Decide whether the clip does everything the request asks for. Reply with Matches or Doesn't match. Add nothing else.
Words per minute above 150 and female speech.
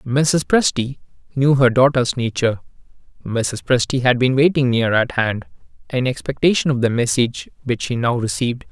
Doesn't match